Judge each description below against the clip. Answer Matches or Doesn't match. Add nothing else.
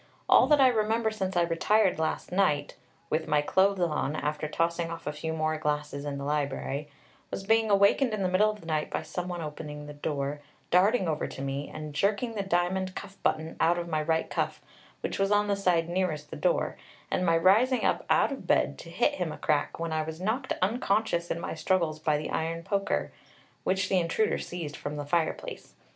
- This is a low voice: Doesn't match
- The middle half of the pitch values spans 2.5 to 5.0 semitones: Matches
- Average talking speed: Doesn't match